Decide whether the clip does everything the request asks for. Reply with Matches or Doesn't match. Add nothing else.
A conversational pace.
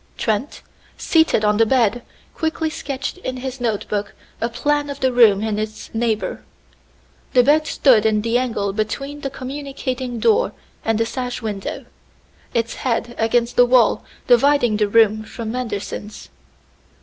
Matches